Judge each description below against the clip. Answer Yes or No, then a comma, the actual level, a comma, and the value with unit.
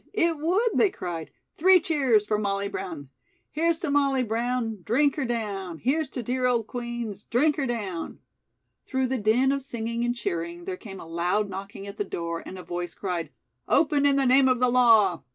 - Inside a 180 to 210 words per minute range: Yes, average, 195 wpm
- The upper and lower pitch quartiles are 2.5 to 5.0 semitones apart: No, wide, 5.6 semitones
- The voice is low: No, high, 235 Hz